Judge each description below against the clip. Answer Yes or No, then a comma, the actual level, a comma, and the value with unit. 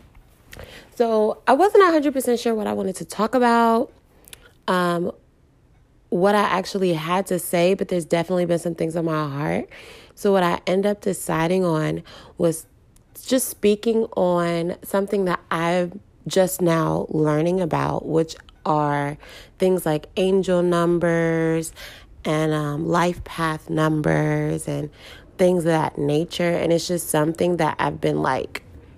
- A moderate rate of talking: Yes, average, 145 wpm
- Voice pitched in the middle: Yes, medium, 175 Hz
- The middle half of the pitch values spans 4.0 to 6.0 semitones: No, average, 3.2 semitones